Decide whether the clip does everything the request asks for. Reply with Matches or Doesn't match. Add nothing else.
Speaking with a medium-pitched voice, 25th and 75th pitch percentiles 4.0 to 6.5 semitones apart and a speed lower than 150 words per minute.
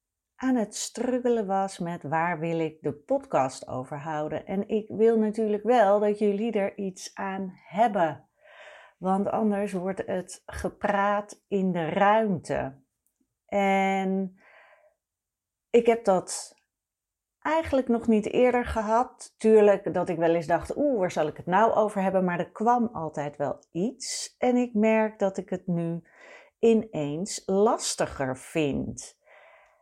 Doesn't match